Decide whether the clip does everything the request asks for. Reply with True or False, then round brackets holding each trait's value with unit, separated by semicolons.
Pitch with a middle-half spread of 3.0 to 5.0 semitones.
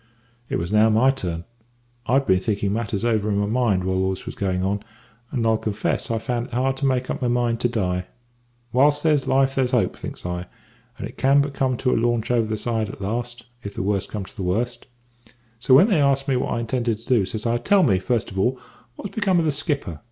True (4.5 semitones)